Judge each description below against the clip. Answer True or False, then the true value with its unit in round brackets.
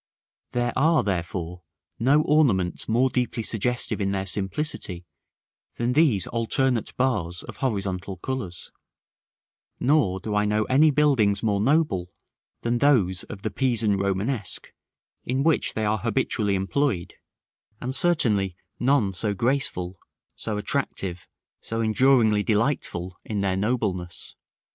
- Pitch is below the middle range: True (110 Hz)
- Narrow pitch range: False (5.2 semitones)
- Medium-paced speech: False (125 wpm)